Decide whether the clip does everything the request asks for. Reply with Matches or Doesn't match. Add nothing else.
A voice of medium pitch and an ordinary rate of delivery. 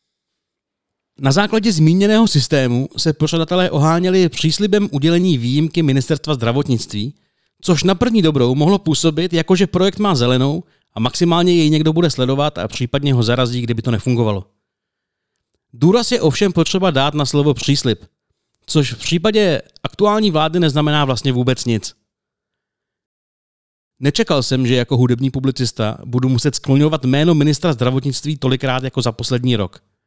Matches